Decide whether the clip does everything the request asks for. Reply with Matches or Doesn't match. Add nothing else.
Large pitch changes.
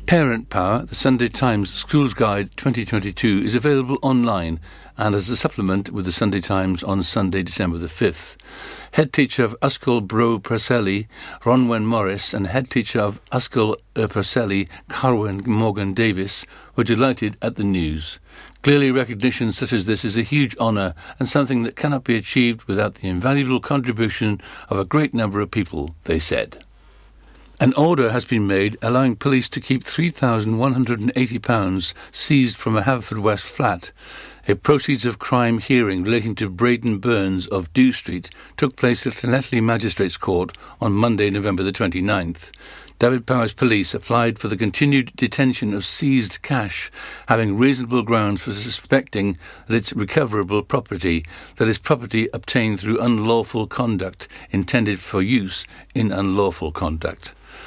Doesn't match